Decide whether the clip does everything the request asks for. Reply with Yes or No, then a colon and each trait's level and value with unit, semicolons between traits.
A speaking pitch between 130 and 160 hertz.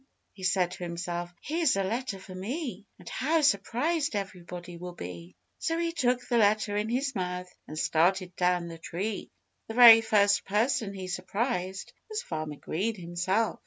No: high, 195 Hz